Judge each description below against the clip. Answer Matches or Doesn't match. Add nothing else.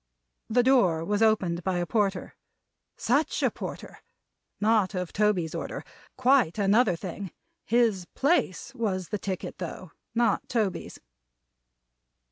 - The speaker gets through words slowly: Matches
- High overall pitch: Matches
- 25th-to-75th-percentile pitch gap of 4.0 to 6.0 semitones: Matches